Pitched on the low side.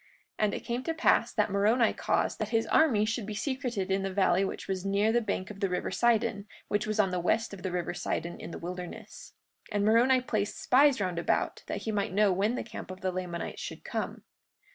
No: high, 205 Hz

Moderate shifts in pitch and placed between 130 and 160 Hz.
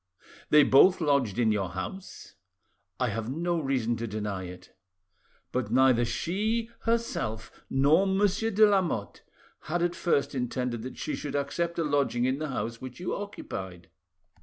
No: wide, 7.0 semitones; medium, 140 Hz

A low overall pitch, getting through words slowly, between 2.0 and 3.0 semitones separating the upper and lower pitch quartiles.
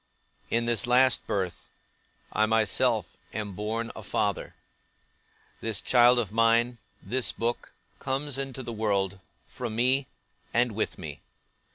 Yes: low, 115 Hz; slow, 130 wpm; narrow, 2.6 semitones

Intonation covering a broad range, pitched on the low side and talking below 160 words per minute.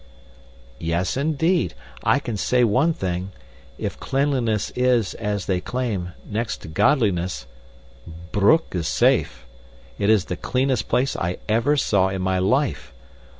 Yes: wide, 6.0 semitones; low, 110 Hz; slow, 135 wpm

